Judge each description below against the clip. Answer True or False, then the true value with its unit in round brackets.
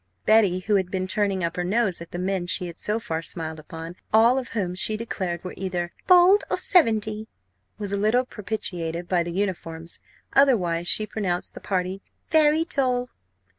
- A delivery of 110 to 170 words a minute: False (180 wpm)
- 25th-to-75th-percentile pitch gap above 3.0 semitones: True (4.1 semitones)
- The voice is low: False (195 Hz)